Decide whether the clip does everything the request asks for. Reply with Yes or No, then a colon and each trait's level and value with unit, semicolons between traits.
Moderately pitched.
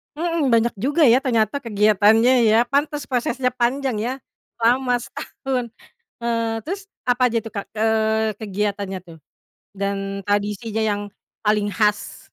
No: high, 225 Hz